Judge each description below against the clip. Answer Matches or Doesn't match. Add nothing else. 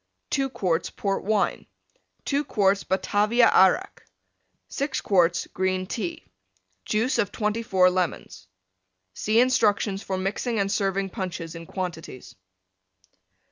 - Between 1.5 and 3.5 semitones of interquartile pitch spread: Matches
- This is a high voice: Matches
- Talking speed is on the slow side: Matches